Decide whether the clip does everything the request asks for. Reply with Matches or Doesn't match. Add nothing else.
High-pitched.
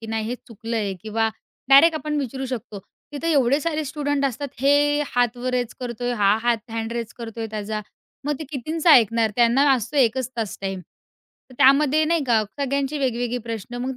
Matches